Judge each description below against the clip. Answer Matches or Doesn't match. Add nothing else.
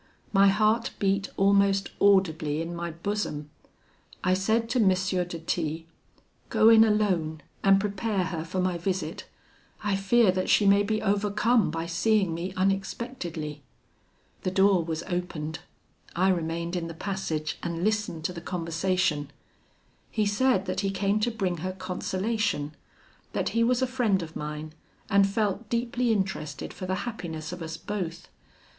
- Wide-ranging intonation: Doesn't match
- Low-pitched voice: Doesn't match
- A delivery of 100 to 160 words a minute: Matches